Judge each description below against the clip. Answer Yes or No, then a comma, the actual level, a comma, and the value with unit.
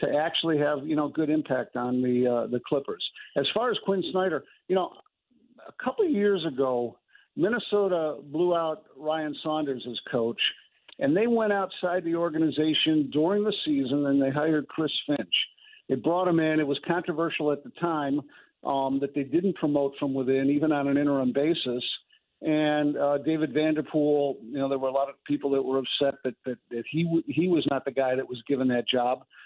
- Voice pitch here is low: No, medium, 150 Hz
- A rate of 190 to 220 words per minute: Yes, average, 200 wpm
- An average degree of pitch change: Yes, average, 3.4 semitones